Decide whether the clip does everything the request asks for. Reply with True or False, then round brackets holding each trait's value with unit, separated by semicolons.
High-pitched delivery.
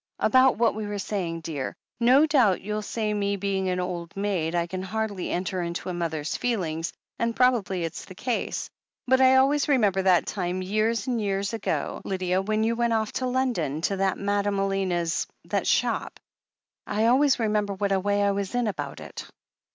True (200 Hz)